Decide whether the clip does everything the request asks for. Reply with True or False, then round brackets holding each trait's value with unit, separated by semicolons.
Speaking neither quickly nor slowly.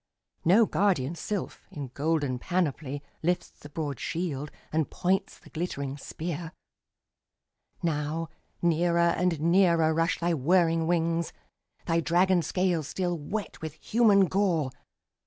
False (120 wpm)